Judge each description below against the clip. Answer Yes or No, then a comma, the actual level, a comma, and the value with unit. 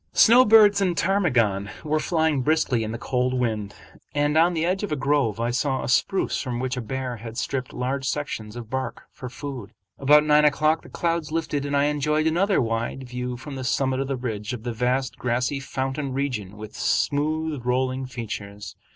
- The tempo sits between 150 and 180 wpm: No, average, 195 wpm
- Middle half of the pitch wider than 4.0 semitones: No, average, 3.7 semitones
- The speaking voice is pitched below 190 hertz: Yes, low, 135 Hz